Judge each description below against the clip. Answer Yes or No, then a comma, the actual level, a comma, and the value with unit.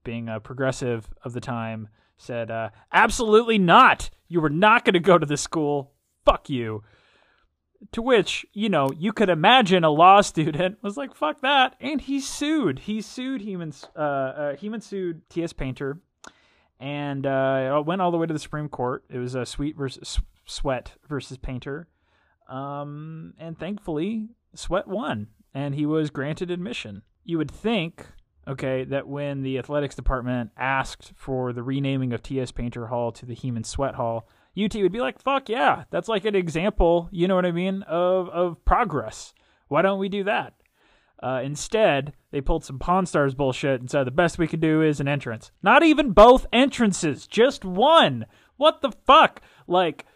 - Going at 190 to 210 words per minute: No, average, 175 wpm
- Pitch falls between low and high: Yes, medium, 155 Hz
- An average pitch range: No, wide, 6.8 semitones